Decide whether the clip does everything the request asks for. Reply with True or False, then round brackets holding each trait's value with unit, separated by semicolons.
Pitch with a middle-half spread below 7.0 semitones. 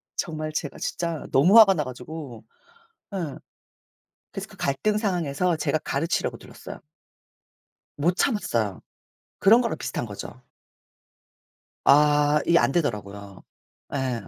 True (5.3 semitones)